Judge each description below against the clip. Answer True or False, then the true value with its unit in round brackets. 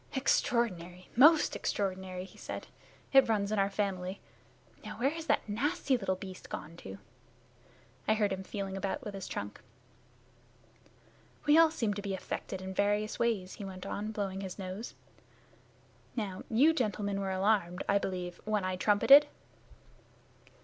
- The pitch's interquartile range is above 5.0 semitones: False (2.9 semitones)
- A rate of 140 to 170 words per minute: True (150 wpm)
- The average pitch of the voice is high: True (200 Hz)